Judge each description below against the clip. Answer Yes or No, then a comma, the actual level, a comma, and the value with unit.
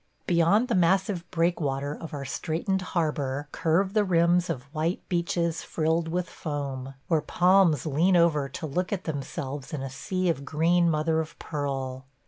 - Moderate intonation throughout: Yes, average, 3.6 semitones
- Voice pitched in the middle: Yes, medium, 165 Hz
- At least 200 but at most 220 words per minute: No, average, 160 wpm